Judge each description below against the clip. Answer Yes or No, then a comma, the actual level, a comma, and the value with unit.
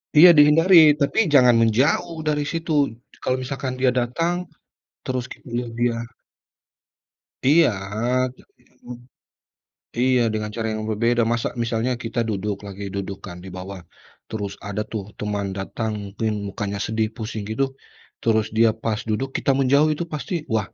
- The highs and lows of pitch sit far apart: No, average, 4.5 semitones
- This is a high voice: No, low, 120 Hz